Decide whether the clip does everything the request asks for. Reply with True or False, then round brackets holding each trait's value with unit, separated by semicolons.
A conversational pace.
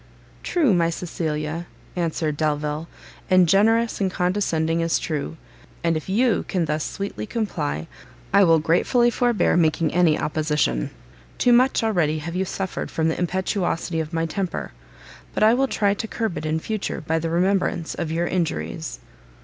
True (160 wpm)